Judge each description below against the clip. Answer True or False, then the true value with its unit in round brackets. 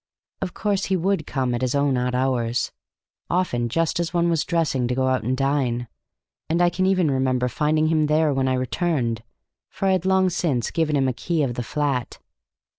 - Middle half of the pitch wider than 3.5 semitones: True (5.0 semitones)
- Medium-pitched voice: True (145 Hz)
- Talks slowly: False (205 wpm)